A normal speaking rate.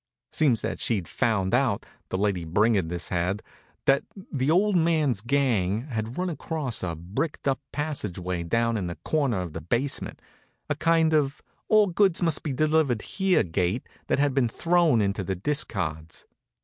Yes: average, 160 wpm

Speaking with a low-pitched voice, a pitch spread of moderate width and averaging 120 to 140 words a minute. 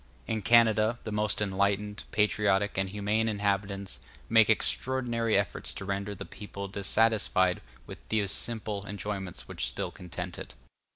No: low, 105 Hz; narrow, 1.9 semitones; slow, 135 wpm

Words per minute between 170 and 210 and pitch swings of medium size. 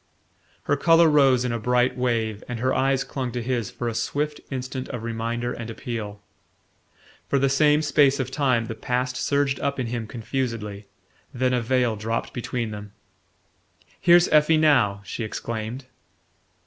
No: average, 160 wpm; average, 3.0 semitones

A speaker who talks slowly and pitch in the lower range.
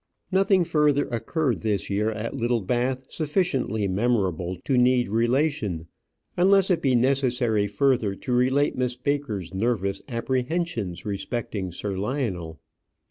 Yes: slow, 120 wpm; low, 120 Hz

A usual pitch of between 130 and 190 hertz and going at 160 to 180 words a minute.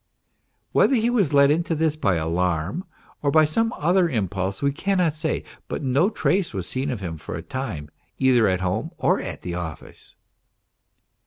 Yes: low, 135 Hz; average, 170 wpm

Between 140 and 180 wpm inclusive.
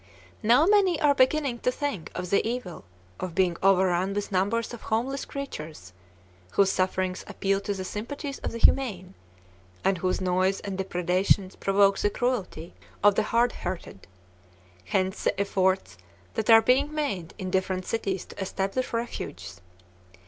Yes: average, 150 wpm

